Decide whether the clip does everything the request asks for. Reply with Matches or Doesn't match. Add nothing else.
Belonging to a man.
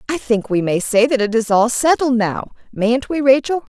Doesn't match